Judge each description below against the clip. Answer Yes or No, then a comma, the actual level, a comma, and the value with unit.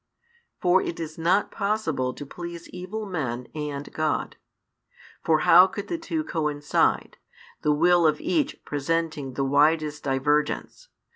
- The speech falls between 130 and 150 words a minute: Yes, slow, 135 wpm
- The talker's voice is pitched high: No, medium, 160 Hz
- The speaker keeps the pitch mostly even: No, average, 3.7 semitones